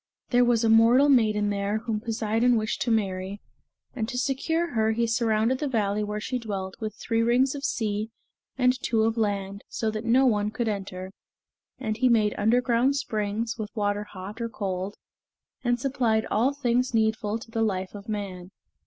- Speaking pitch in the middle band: No, high, 220 Hz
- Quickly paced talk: No, average, 180 wpm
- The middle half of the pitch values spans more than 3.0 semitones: No, narrow, 2.6 semitones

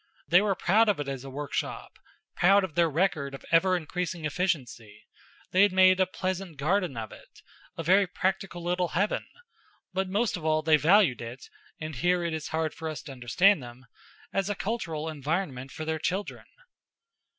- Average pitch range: Yes, average, 4.2 semitones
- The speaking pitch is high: No, medium, 170 Hz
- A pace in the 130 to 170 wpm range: No, average, 185 wpm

